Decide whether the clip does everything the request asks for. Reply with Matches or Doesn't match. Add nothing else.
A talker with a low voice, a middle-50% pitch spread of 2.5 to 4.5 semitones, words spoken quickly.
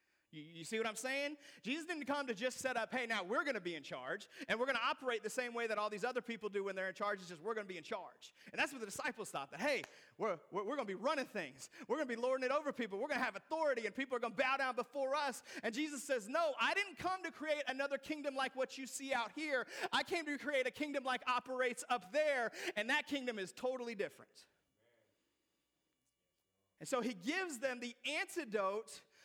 Doesn't match